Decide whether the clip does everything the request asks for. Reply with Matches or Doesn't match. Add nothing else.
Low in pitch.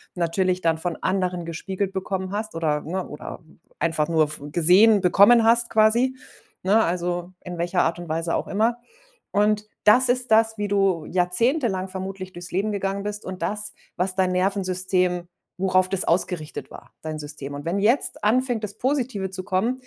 Doesn't match